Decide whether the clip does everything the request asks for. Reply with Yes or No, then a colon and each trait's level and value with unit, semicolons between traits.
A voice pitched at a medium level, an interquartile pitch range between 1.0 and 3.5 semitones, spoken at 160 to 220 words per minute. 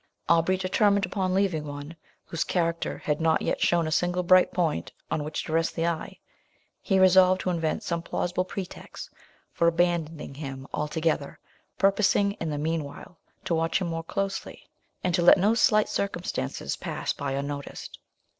Yes: medium, 170 Hz; average, 2.8 semitones; average, 165 wpm